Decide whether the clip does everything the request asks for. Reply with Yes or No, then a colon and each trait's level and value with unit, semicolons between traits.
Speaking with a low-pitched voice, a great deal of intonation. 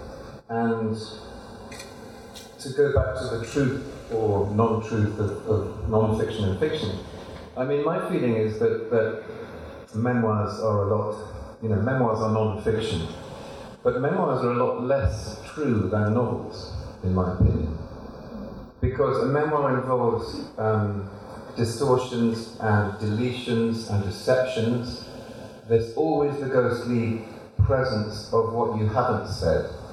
No: low, 110 Hz; narrow, 2.4 semitones